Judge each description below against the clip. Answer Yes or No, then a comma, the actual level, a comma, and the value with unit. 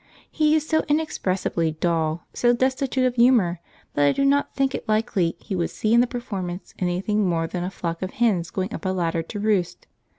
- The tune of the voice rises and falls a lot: Yes, wide, 5.9 semitones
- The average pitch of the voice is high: Yes, high, 195 Hz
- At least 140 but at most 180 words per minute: No, fast, 205 wpm